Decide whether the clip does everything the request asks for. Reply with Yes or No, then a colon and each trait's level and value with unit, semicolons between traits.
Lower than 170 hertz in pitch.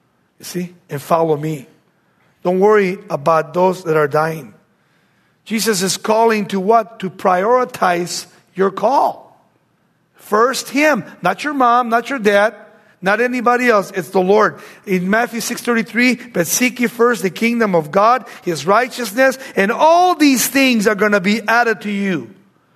No: high, 210 Hz